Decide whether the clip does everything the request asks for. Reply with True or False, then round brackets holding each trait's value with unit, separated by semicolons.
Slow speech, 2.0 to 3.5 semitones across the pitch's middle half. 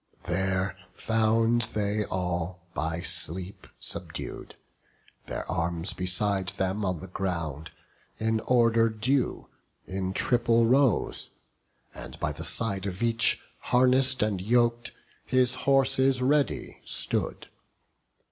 False (110 wpm; 4.4 semitones)